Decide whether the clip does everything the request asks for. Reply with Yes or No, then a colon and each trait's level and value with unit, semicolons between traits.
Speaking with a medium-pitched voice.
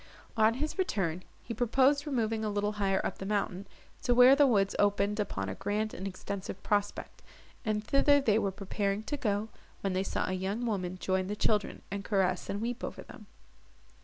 No: high, 205 Hz